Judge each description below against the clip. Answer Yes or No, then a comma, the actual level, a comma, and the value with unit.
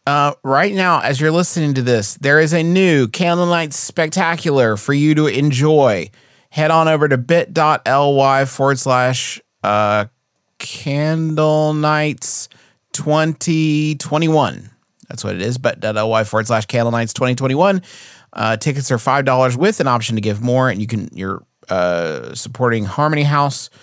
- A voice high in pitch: No, medium, 140 Hz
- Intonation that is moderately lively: Yes, average, 3.9 semitones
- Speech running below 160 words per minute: Yes, average, 150 wpm